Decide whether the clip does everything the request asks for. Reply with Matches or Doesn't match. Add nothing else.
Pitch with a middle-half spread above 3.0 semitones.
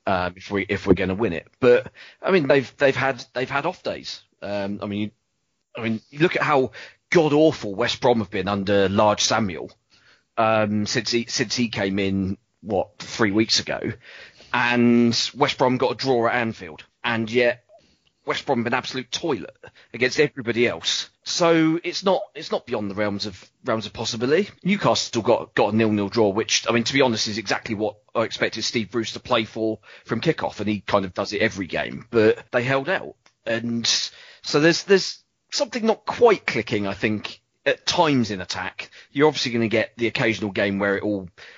Matches